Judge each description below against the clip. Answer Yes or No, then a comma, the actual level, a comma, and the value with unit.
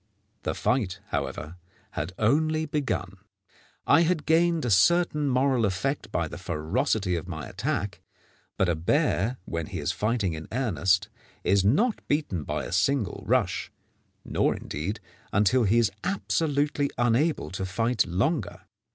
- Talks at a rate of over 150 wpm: No, average, 145 wpm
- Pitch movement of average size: No, wide, 7.6 semitones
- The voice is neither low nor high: No, low, 105 Hz